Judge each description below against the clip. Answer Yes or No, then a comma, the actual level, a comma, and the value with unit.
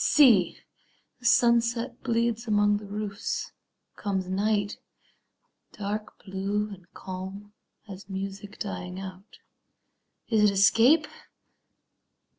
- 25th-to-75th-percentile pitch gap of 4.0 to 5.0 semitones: No, average, 2.8 semitones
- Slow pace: Yes, slow, 95 wpm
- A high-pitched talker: Yes, high, 205 Hz